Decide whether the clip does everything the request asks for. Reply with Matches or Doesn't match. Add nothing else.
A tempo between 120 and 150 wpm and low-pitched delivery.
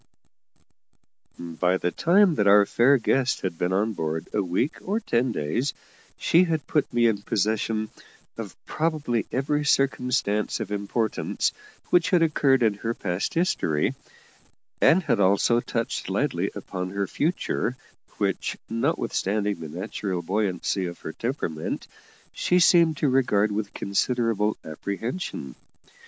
Matches